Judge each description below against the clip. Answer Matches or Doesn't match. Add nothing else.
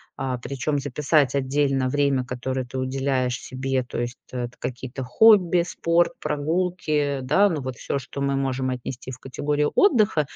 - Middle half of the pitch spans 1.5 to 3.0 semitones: Matches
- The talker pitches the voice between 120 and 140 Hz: Matches